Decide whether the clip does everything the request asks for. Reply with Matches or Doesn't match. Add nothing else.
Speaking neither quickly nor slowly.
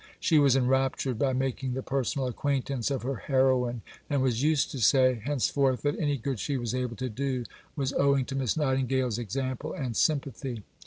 Matches